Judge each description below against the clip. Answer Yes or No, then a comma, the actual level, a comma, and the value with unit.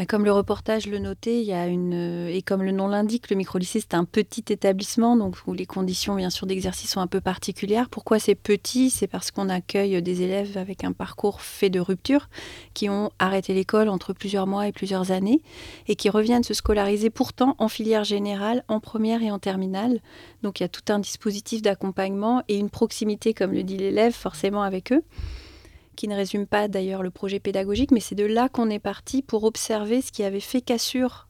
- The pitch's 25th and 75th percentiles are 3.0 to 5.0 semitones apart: No, narrow, 2.5 semitones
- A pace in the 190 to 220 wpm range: Yes, average, 210 wpm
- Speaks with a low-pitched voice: No, high, 205 Hz